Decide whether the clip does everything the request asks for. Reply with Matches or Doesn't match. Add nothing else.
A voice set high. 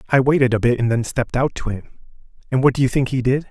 Doesn't match